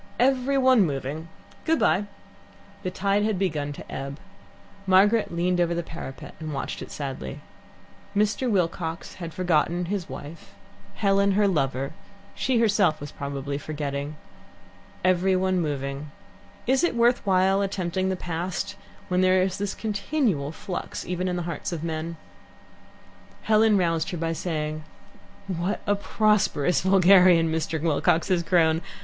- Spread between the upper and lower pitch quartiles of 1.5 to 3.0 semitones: No, average, 4.0 semitones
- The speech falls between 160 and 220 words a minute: No, average, 145 wpm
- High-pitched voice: No, medium, 180 Hz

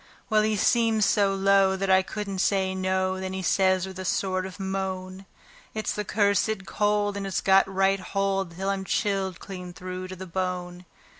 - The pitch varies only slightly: Yes, narrow, 1.0 semitones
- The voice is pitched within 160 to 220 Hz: Yes, high, 190 Hz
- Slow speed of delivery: No, average, 190 wpm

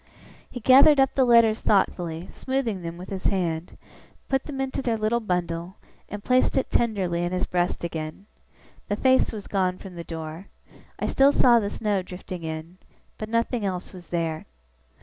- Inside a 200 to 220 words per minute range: No, average, 175 wpm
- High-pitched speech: Yes, high, 195 Hz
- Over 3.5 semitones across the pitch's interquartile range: Yes, average, 5.2 semitones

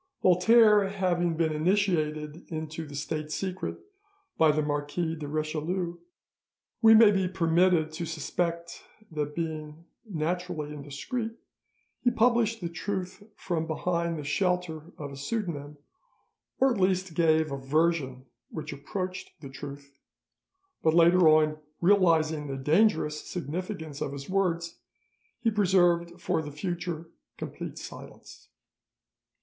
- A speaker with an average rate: No, slow, 125 wpm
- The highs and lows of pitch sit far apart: No, average, 3.3 semitones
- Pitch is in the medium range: Yes, medium, 165 Hz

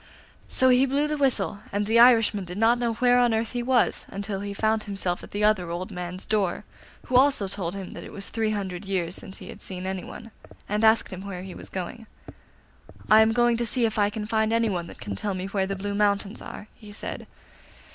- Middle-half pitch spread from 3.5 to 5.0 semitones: No, average, 3.0 semitones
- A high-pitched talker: Yes, high, 210 Hz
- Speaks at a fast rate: Yes, fast, 230 wpm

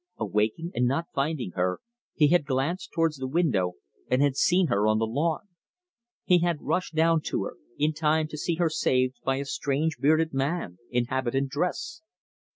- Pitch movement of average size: Yes, average, 4.2 semitones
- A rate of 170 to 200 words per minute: Yes, average, 180 wpm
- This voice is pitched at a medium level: Yes, medium, 145 Hz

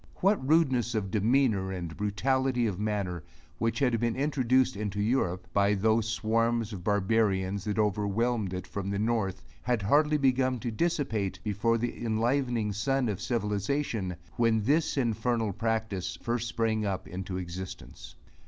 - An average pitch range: Yes, average, 3.4 semitones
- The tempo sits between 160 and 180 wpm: No, average, 145 wpm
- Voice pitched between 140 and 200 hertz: No, low, 110 Hz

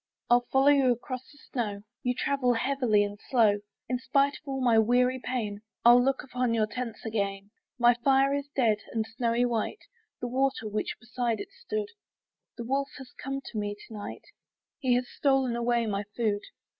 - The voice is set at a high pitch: Yes, high, 245 Hz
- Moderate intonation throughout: Yes, average, 3.1 semitones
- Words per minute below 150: No, average, 185 wpm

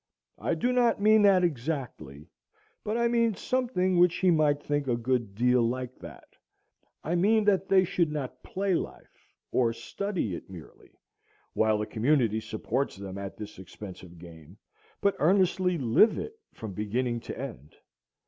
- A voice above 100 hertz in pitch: Yes, medium, 140 Hz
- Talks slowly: No, average, 160 wpm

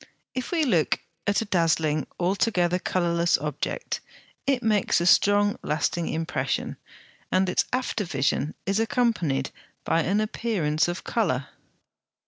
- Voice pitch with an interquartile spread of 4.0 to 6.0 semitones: Yes, average, 4.9 semitones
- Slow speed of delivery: Yes, slow, 125 wpm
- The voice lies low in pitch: No, medium, 180 Hz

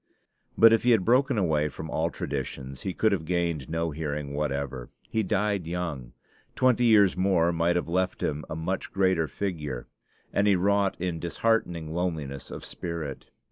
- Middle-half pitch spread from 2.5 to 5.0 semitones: Yes, average, 4.2 semitones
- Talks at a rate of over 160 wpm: Yes, average, 170 wpm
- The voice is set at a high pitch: No, very low, 85 Hz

